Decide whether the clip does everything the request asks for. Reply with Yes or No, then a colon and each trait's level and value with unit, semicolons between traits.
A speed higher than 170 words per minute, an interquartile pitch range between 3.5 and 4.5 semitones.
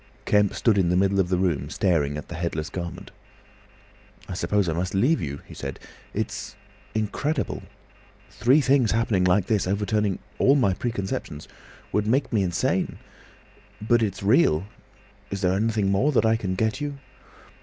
No: average, 155 wpm; average, 3.9 semitones